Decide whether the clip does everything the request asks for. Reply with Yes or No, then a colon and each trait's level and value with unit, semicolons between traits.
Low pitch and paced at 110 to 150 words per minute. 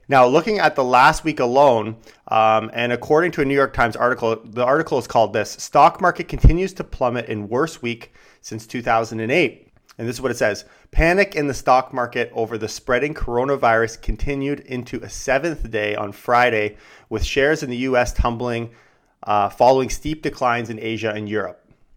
No: low, 120 Hz; average, 185 wpm